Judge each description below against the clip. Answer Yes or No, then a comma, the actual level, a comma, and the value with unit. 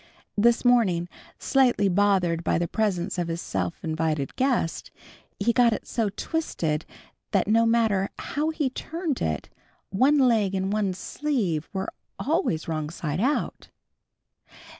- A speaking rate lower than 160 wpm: Yes, average, 140 wpm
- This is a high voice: Yes, high, 200 Hz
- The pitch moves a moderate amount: No, wide, 6.5 semitones